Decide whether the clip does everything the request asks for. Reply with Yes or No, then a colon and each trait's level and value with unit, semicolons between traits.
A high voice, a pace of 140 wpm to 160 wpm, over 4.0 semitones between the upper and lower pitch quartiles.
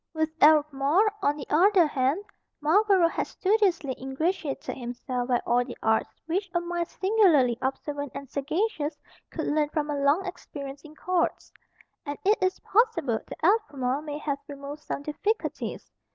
Yes: very high, 300 Hz; average, 150 wpm; average, 4.7 semitones